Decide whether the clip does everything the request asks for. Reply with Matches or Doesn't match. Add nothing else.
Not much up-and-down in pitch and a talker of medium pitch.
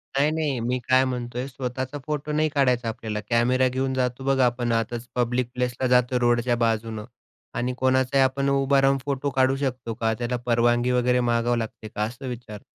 Doesn't match